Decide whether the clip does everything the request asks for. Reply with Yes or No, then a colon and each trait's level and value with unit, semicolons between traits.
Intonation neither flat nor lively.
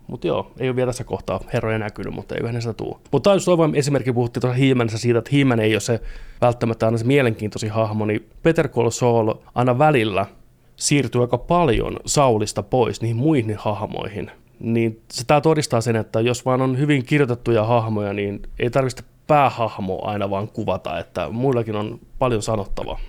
Yes: average, 3.1 semitones